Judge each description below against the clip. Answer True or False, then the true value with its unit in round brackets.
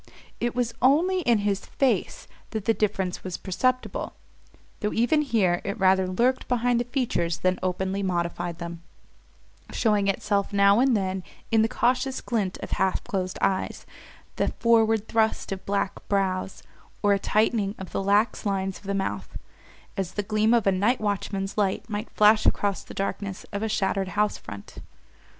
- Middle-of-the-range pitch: False (200 Hz)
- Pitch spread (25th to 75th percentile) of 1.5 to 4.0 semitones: True (2.9 semitones)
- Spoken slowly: False (170 wpm)